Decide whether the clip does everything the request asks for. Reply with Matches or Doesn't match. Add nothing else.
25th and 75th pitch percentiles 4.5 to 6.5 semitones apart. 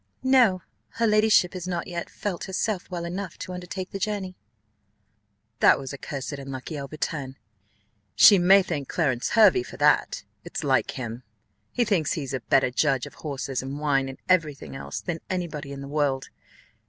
Matches